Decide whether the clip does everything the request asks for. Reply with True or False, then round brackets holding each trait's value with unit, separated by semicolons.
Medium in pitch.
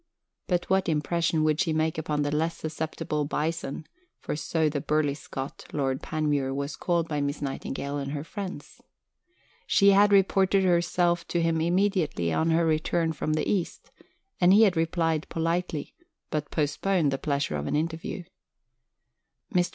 True (160 Hz)